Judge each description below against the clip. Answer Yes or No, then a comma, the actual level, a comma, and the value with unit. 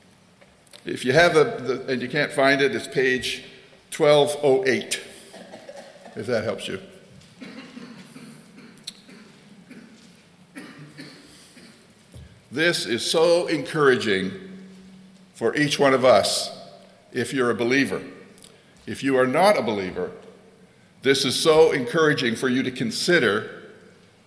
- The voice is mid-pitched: Yes, medium, 155 Hz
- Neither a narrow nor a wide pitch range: No, wide, 7.9 semitones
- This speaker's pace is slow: Yes, slow, 110 wpm